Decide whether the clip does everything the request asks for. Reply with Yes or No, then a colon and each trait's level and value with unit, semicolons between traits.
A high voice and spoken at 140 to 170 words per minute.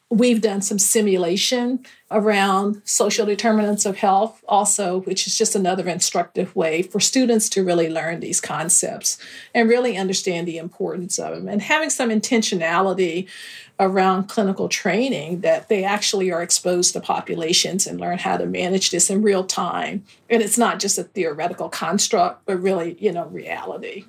Yes: high, 195 Hz; average, 160 wpm